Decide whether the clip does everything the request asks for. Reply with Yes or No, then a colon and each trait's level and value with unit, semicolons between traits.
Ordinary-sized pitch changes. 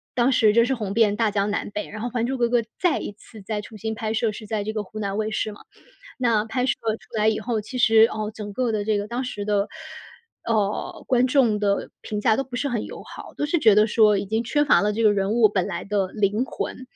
No: narrow, 2.3 semitones